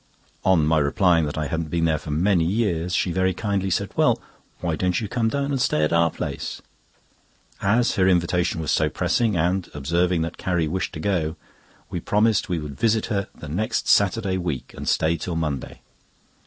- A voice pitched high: No, very low, 90 Hz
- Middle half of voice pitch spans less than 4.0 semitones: Yes, average, 3.5 semitones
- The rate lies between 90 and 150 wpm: No, average, 195 wpm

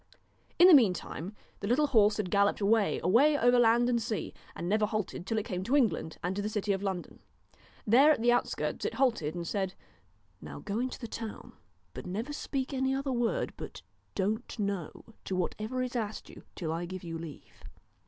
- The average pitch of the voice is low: No, high, 215 Hz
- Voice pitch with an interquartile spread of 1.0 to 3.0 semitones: No, average, 4.5 semitones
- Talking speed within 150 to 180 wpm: No, average, 200 wpm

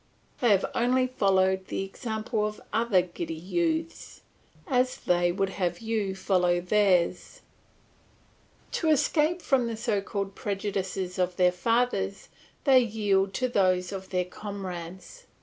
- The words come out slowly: Yes, slow, 130 wpm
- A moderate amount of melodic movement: Yes, average, 4.2 semitones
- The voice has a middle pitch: No, high, 200 Hz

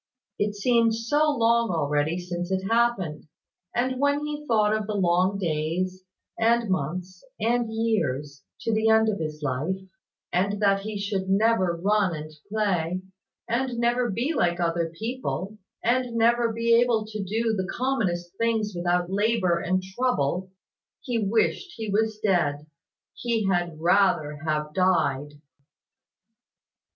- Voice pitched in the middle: No, high, 200 Hz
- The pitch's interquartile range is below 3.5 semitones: No, average, 4.7 semitones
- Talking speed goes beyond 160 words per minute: No, average, 140 wpm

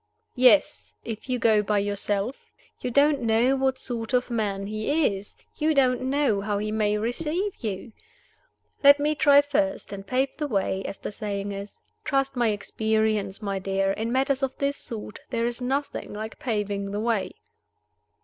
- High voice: Yes, high, 230 Hz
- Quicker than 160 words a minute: Yes, average, 170 wpm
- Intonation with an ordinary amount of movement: Yes, average, 4.8 semitones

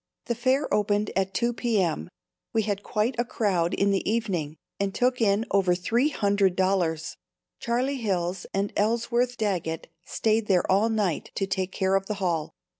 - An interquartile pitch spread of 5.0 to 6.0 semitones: No, average, 3.4 semitones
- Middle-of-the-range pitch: No, high, 200 Hz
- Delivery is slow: No, average, 170 wpm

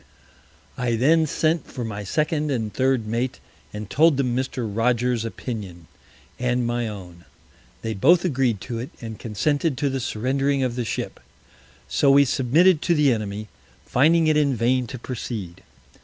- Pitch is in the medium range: No, low, 125 Hz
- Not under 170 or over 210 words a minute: No, average, 160 wpm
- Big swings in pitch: No, average, 4.0 semitones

